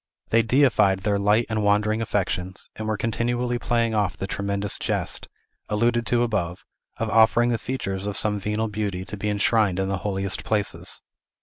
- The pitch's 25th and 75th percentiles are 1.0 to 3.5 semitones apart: Yes, narrow, 2.4 semitones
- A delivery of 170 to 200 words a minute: Yes, average, 175 wpm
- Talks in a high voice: No, low, 105 Hz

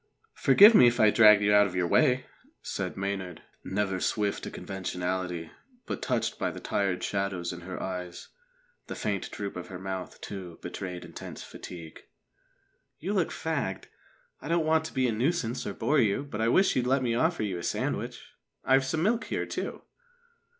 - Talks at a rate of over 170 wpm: Yes, average, 185 wpm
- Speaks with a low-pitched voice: Yes, low, 105 Hz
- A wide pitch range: Yes, wide, 6.2 semitones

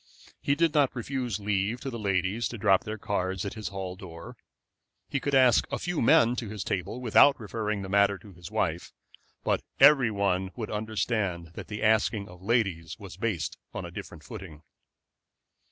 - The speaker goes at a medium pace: Yes, average, 185 wpm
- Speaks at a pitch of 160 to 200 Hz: No, low, 105 Hz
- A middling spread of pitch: Yes, average, 3.7 semitones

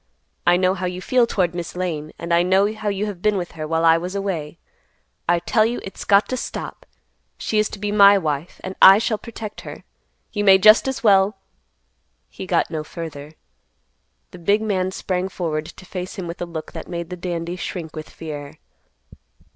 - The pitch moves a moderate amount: Yes, average, 3.2 semitones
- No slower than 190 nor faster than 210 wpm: Yes, average, 200 wpm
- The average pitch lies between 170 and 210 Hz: Yes, medium, 185 Hz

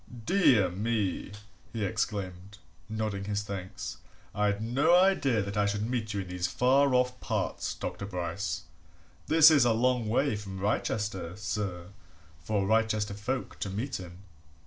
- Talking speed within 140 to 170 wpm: Yes, average, 145 wpm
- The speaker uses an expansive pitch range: No, average, 3.8 semitones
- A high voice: No, low, 105 Hz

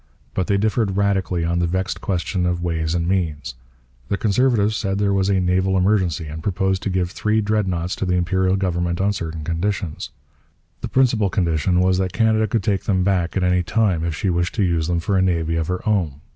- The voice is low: Yes, very low, 95 Hz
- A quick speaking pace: Yes, fast, 215 wpm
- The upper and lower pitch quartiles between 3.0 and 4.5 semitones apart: No, narrow, 2.5 semitones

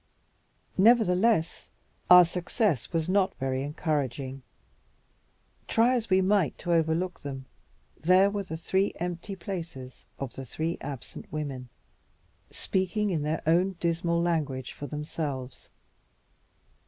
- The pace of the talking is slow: Yes, slow, 115 wpm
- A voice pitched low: No, medium, 170 Hz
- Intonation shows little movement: No, average, 4.5 semitones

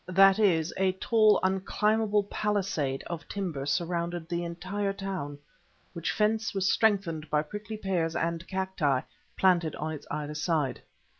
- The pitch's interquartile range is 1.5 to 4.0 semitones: Yes, average, 3.7 semitones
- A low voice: No, medium, 185 Hz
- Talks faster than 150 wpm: No, average, 140 wpm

